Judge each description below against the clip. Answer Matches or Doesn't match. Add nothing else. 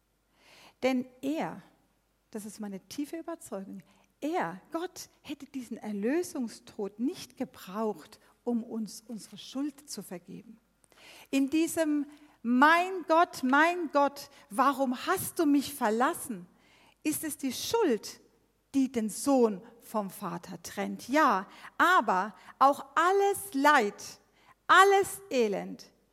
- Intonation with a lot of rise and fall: Matches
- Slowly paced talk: Matches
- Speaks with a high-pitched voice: Matches